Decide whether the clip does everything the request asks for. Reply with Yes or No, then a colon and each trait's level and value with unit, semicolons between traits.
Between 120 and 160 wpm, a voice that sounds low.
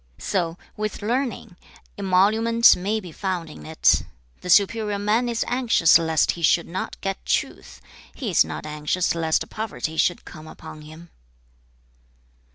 No: average, 145 wpm; medium, 185 Hz